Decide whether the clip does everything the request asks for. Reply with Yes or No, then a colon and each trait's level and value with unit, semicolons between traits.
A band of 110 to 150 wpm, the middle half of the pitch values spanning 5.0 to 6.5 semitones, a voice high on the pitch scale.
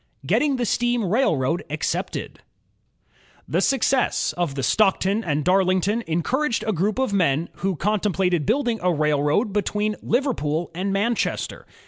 Yes: slow, 135 wpm; average, 5.3 semitones; high, 195 Hz